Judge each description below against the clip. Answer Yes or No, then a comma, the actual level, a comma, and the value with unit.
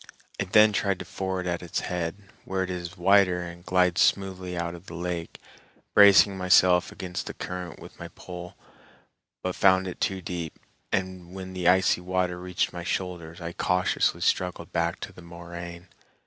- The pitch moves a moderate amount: No, narrow, 1.3 semitones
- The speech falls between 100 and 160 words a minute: No, average, 175 wpm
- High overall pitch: No, very low, 90 Hz